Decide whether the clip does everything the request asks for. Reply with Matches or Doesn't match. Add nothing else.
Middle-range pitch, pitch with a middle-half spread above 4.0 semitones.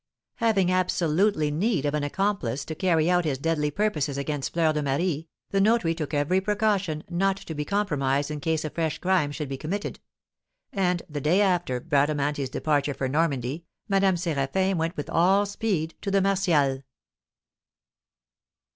Matches